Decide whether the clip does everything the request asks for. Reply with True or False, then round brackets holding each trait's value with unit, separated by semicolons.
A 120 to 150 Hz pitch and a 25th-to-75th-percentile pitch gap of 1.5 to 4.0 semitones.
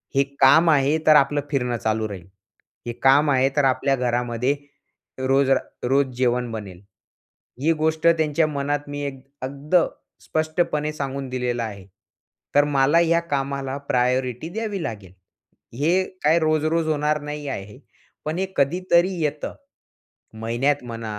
True (140 Hz; 3.7 semitones)